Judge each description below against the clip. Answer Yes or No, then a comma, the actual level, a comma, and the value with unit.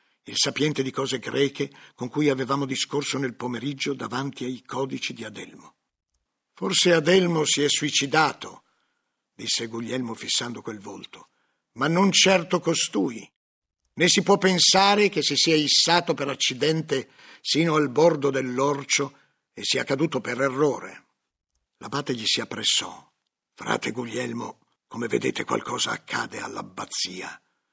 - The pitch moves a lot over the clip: No, average, 3.9 semitones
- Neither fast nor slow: Yes, average, 130 wpm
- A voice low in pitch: No, medium, 145 Hz